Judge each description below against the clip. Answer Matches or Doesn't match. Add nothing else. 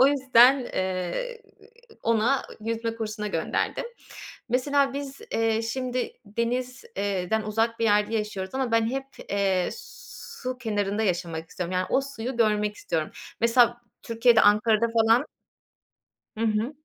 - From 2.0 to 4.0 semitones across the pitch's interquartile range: Matches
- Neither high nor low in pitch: Doesn't match